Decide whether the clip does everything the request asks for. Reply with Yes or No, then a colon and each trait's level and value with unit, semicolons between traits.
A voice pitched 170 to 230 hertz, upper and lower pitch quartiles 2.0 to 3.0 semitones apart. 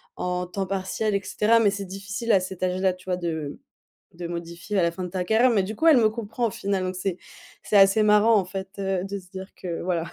Yes: high, 190 Hz; narrow, 2.4 semitones